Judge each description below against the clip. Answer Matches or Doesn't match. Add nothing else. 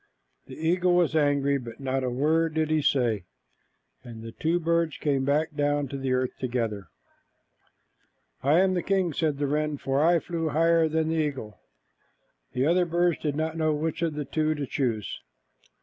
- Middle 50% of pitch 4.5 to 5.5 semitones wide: Doesn't match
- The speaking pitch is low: Doesn't match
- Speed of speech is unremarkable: Matches